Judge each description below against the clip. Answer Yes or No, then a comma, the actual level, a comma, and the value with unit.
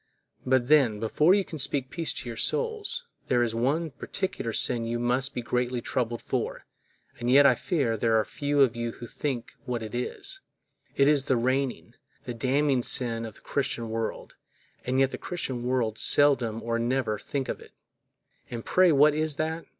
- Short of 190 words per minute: Yes, average, 180 wpm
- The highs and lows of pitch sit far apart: No, average, 3.7 semitones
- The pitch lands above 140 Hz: No, low, 130 Hz